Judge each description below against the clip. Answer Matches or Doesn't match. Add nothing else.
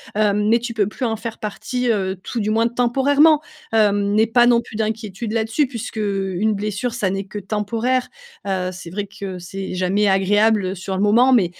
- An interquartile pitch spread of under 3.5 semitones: Matches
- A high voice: Matches